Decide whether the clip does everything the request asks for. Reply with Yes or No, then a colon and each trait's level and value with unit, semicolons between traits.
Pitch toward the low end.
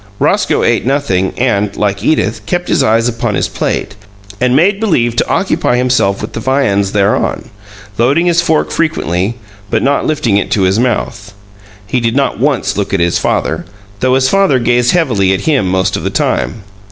Yes: low, 120 Hz